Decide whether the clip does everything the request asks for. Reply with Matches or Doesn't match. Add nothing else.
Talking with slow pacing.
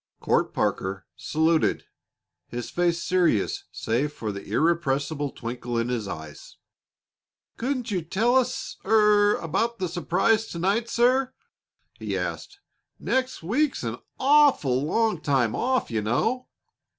Matches